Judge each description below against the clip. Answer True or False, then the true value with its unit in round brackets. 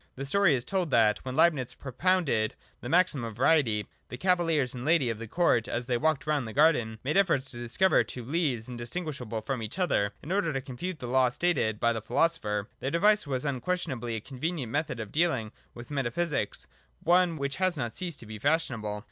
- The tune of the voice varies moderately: False (6.0 semitones)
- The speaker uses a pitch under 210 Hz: True (135 Hz)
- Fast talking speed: True (210 wpm)